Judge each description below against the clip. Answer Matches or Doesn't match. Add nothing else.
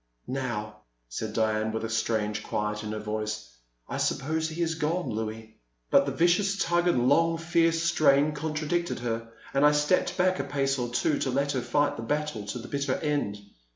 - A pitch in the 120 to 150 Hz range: Matches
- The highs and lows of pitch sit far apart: Matches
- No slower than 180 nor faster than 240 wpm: Matches